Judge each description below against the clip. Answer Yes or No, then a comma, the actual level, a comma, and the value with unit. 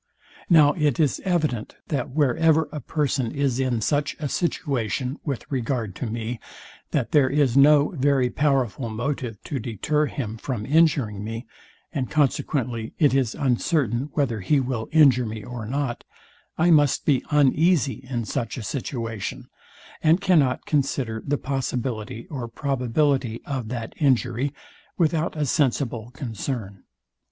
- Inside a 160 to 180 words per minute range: No, average, 140 wpm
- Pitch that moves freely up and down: No, average, 3.9 semitones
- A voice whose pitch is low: Yes, low, 130 Hz